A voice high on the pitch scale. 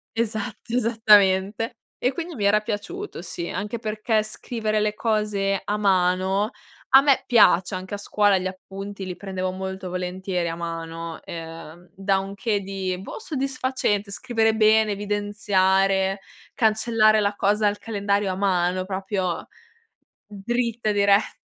Yes: high, 200 Hz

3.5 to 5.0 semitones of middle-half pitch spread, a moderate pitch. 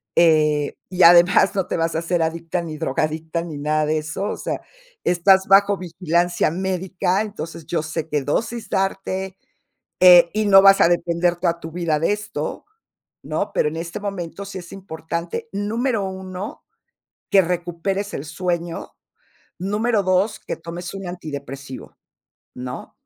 No: average, 3.0 semitones; medium, 175 Hz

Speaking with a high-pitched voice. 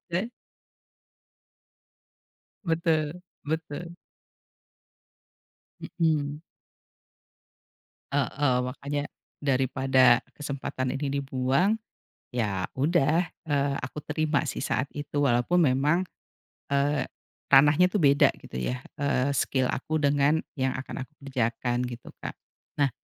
No: medium, 140 Hz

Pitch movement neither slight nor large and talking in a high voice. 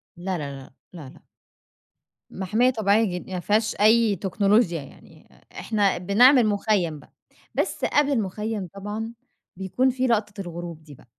Yes: average, 3.9 semitones; high, 205 Hz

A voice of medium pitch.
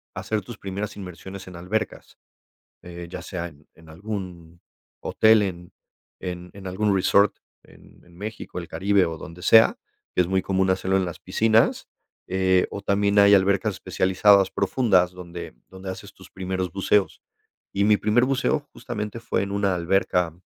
No: very low, 95 Hz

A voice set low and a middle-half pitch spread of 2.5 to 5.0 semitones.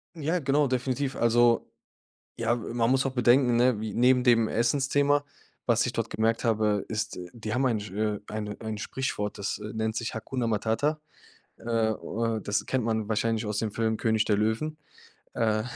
Yes: low, 115 Hz; average, 2.9 semitones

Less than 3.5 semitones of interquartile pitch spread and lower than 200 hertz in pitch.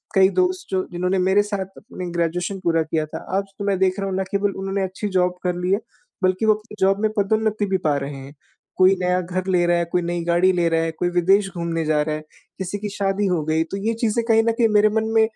Yes: average, 2.9 semitones; high, 190 Hz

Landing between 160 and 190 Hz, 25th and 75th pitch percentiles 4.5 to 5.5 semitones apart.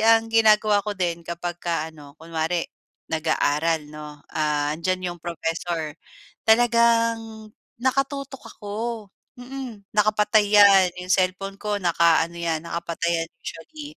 Yes: medium, 185 Hz; average, 5.0 semitones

